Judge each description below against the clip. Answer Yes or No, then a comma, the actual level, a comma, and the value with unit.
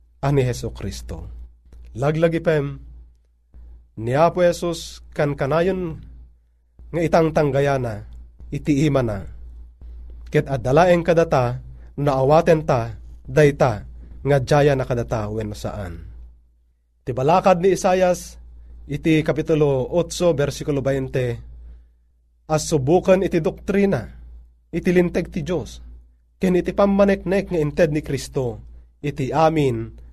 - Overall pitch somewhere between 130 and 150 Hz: Yes, low, 135 Hz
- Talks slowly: Yes, slow, 105 wpm